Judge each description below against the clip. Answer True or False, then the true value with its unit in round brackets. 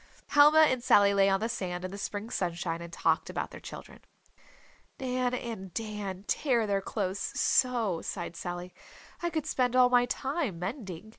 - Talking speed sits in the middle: True (170 wpm)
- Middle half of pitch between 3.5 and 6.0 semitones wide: True (5.2 semitones)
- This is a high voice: True (210 Hz)